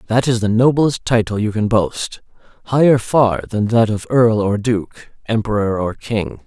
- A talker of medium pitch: No, low, 110 Hz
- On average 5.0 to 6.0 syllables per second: No, 4.4 syllables/s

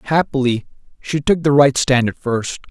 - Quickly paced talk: No, average, 175 wpm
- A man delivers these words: Yes, male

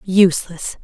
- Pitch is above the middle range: No, medium, 180 Hz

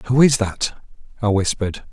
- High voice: No, low, 110 Hz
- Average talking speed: Yes, average, 155 wpm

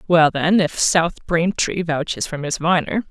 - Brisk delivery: No, average, 175 wpm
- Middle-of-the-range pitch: Yes, medium, 165 Hz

